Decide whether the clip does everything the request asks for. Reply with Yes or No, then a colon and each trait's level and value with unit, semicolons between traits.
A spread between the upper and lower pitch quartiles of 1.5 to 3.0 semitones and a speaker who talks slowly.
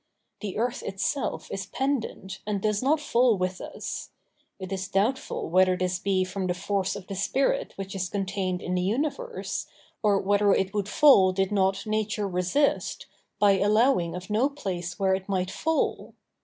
No: average, 2.7 semitones; average, 170 wpm